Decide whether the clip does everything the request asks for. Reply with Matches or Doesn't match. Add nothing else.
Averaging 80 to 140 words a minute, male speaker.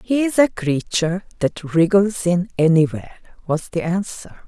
Doesn't match